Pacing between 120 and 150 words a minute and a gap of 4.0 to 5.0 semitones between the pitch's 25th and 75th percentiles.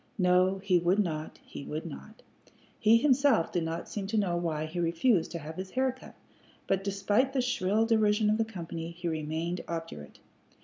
No: average, 185 wpm; average, 4.4 semitones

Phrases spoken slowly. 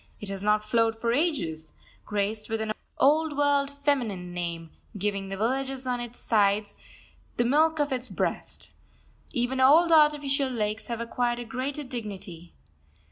No: average, 150 wpm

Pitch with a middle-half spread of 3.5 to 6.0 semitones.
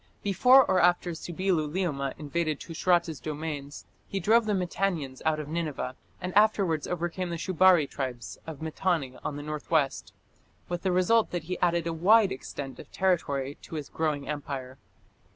Yes: average, 4.0 semitones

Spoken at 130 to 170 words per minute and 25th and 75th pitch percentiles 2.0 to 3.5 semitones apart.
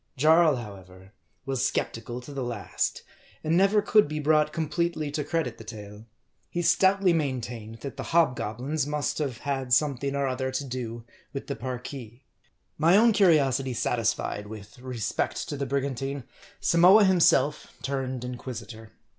No: average, 155 wpm; average, 4.3 semitones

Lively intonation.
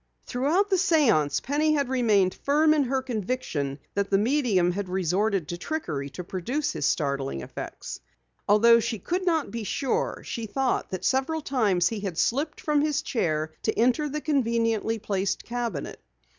Yes: wide, 7.2 semitones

